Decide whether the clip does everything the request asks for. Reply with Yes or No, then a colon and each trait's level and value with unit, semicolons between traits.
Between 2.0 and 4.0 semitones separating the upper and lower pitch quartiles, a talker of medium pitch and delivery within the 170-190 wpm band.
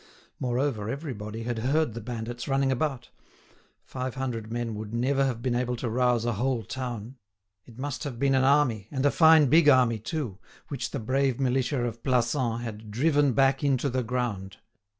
No: average, 2.8 semitones; low, 125 Hz; average, 180 wpm